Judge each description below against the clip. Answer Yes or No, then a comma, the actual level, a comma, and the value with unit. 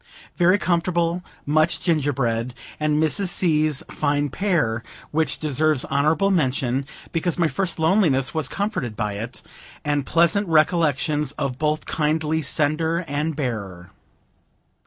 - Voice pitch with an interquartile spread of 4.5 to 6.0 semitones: No, average, 3.5 semitones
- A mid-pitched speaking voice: Yes, medium, 155 Hz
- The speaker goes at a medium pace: No, slow, 120 wpm